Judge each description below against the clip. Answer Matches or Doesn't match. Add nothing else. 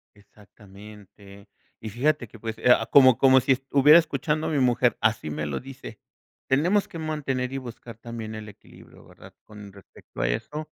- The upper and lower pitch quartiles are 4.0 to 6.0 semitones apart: Matches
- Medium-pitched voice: Doesn't match